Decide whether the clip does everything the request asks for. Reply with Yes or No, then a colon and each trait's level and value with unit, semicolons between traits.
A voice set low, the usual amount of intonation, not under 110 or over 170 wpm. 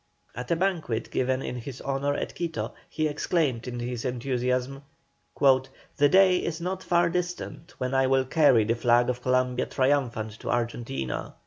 Yes: low, 130 Hz; average, 4.2 semitones; average, 160 wpm